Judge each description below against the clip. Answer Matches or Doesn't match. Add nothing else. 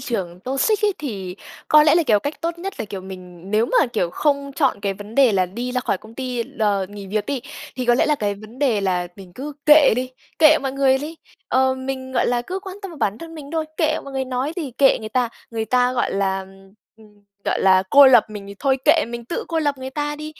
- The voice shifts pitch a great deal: Matches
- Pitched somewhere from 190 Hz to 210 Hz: Doesn't match